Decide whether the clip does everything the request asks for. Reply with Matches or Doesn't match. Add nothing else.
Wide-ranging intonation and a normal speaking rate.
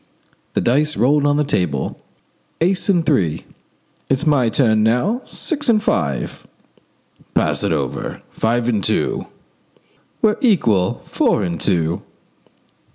Doesn't match